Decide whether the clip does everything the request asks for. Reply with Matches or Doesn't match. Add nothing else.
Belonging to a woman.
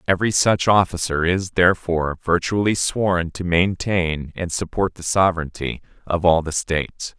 Doesn't match